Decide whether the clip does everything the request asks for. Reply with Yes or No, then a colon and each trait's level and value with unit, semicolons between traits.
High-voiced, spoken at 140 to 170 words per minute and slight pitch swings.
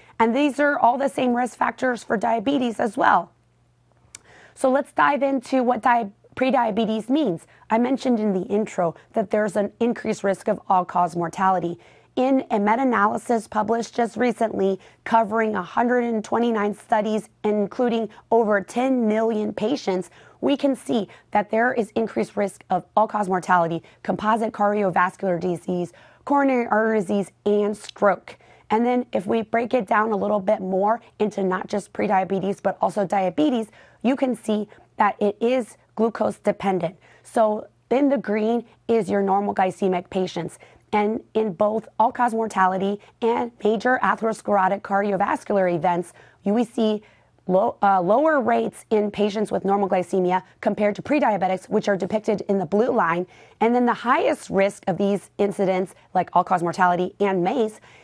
No: high, 210 Hz; average, 155 wpm; average, 3.2 semitones